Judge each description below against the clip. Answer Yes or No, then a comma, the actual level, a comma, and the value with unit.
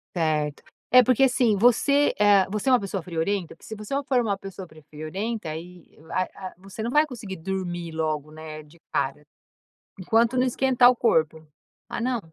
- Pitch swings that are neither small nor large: No, wide, 6.7 semitones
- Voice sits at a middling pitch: No, high, 195 Hz